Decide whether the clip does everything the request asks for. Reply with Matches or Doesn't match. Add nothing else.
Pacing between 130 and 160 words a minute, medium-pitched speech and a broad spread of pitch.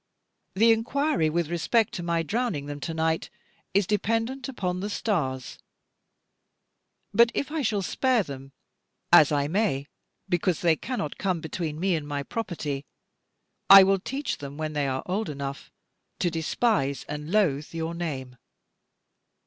Matches